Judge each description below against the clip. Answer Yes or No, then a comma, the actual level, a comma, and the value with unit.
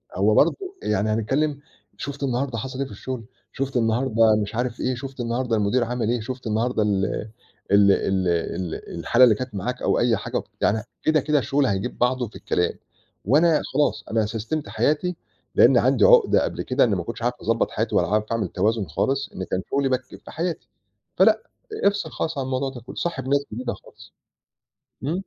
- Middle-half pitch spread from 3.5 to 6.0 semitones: Yes, average, 4.0 semitones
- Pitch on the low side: Yes, low, 125 Hz